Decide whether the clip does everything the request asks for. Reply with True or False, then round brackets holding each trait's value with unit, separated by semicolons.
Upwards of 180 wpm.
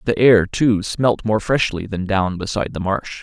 True (205 wpm)